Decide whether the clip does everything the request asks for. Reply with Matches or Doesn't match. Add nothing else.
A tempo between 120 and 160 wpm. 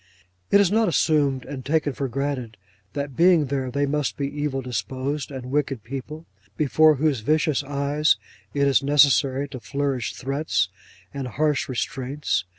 Matches